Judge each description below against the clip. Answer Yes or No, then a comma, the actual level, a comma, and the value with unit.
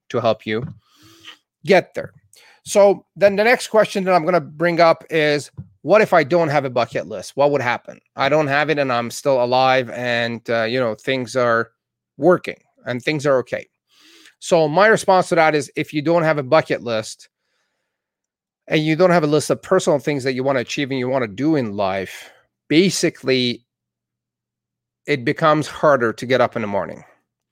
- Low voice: No, medium, 145 Hz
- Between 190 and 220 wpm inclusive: Yes, average, 200 wpm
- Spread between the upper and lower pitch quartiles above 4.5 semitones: Yes, average, 4.9 semitones